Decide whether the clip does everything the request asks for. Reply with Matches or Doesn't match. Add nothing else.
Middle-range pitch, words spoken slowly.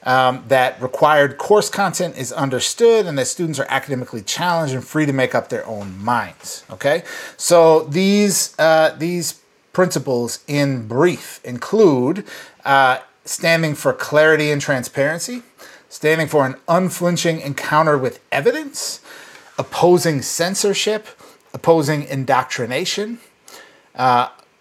Matches